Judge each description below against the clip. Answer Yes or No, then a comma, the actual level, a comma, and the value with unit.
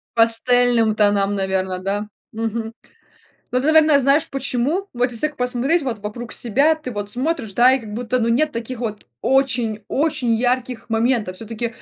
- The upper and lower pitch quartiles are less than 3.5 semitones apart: Yes, average, 3.0 semitones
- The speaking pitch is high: Yes, high, 240 Hz